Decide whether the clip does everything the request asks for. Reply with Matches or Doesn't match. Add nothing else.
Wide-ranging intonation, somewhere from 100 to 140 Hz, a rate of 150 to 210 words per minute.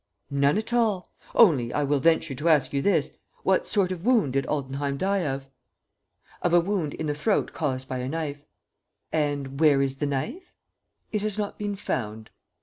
Doesn't match